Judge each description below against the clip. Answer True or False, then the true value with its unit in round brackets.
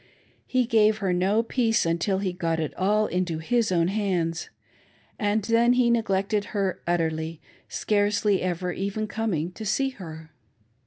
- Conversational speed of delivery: True (150 wpm)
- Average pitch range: True (3.9 semitones)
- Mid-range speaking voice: False (195 Hz)